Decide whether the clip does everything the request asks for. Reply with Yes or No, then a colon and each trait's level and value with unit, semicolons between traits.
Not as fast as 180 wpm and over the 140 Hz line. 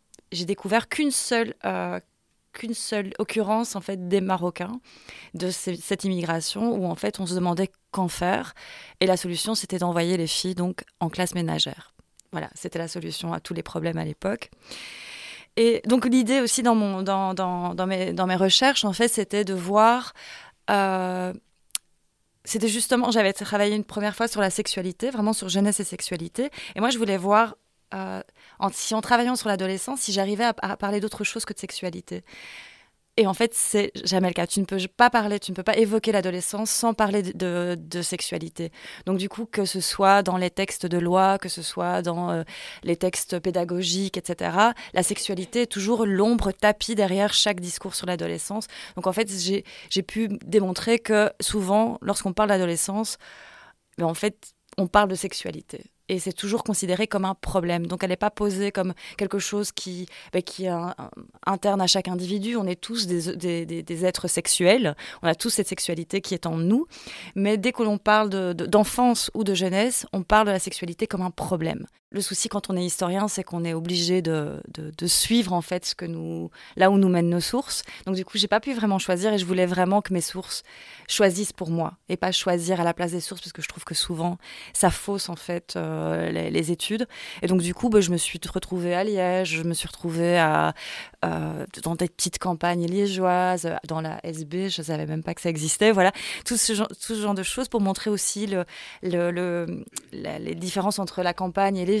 No: average, 210 wpm; high, 190 Hz